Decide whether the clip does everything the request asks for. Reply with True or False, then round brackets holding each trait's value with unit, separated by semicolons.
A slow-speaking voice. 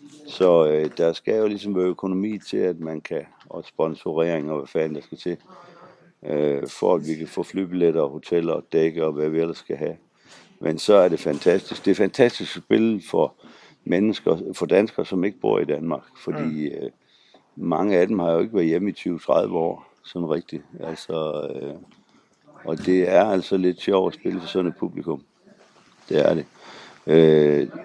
False (190 wpm)